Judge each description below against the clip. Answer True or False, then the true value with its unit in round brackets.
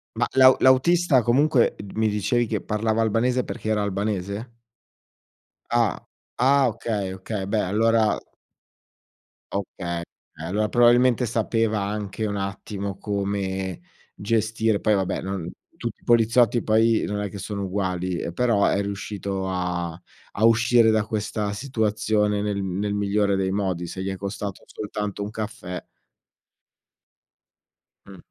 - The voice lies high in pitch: False (105 Hz)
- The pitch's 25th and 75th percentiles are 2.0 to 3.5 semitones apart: True (2.5 semitones)